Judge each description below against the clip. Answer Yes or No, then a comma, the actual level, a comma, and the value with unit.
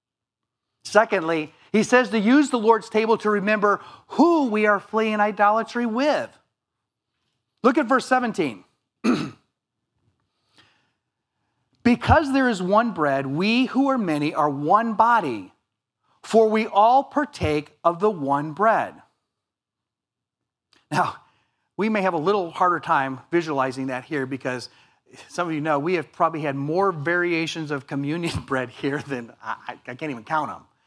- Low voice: No, medium, 180 Hz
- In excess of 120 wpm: Yes, average, 140 wpm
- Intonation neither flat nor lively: No, wide, 7.9 semitones